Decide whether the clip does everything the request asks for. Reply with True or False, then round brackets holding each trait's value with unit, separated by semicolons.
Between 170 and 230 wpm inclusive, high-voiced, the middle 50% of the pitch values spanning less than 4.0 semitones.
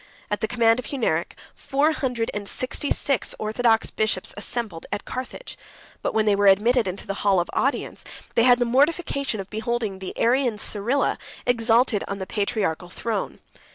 True (175 wpm; 225 Hz; 3.5 semitones)